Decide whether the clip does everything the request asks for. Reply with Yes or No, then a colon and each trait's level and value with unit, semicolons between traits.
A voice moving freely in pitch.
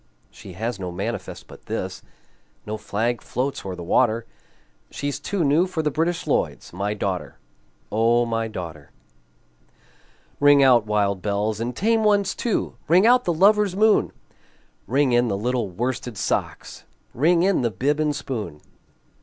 Yes: wide, 7.2 semitones